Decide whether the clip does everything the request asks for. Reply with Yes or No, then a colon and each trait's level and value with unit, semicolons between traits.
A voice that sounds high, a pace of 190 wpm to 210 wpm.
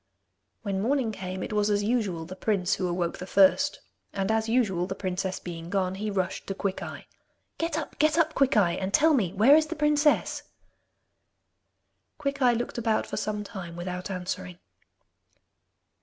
No: high, 200 Hz; average, 165 wpm